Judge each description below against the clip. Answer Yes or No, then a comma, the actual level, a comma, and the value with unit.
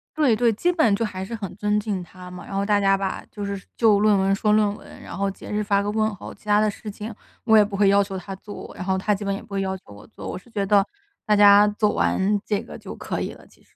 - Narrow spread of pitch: Yes, narrow, 1.3 semitones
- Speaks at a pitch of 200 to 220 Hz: Yes, high, 205 Hz